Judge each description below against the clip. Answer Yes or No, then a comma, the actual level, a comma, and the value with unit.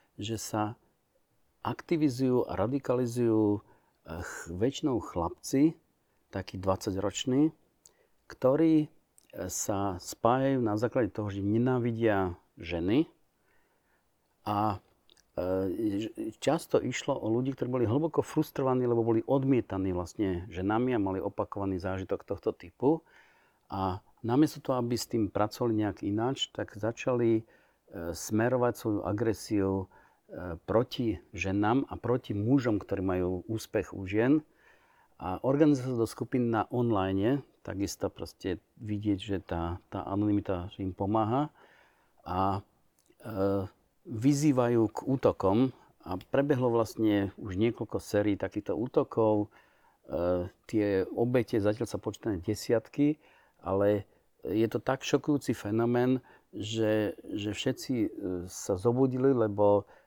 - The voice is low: Yes, low, 110 Hz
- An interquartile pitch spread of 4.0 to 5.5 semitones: Yes, average, 4.4 semitones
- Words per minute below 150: Yes, slow, 110 wpm